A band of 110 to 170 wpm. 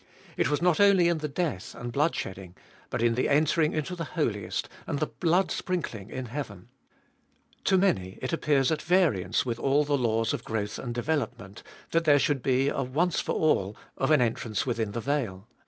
No: average, 195 wpm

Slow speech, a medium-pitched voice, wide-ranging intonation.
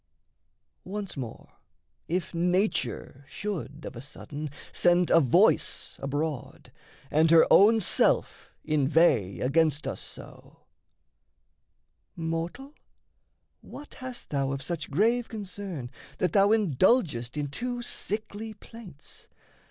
Yes: slow, 105 wpm; medium, 165 Hz; wide, 6.4 semitones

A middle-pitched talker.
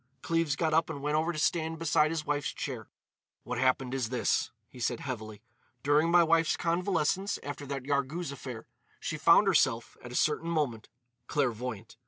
Yes: medium, 145 Hz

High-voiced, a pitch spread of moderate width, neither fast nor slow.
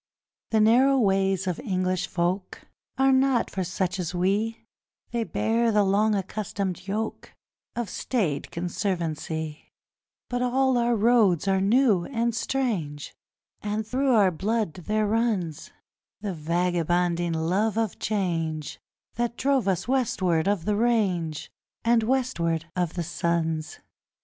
No: high, 195 Hz; average, 4.8 semitones; slow, 130 wpm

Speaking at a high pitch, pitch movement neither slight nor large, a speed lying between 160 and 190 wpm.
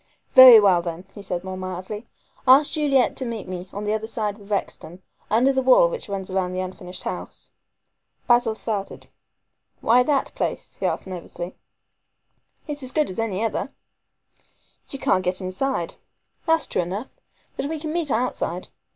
No: high, 210 Hz; wide, 5.7 semitones; average, 170 wpm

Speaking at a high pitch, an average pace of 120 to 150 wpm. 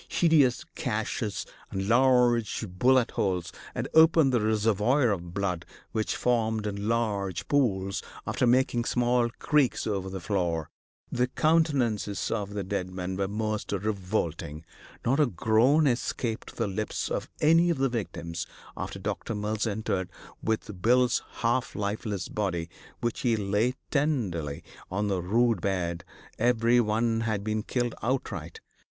No: low, 110 Hz; average, 140 wpm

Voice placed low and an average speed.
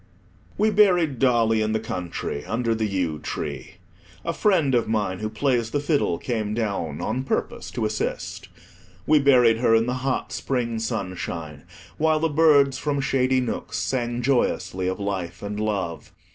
Yes: low, 115 Hz; average, 160 wpm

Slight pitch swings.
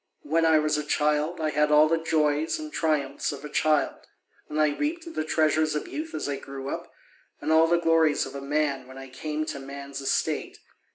Yes: narrow, 2.1 semitones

